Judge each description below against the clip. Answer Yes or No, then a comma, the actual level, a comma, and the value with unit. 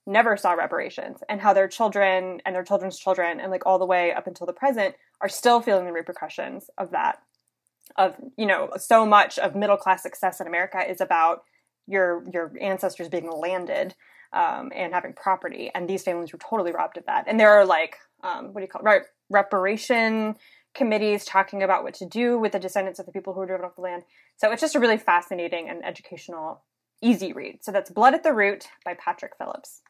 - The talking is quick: Yes, fast, 215 wpm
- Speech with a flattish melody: No, average, 3.1 semitones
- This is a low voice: No, high, 195 Hz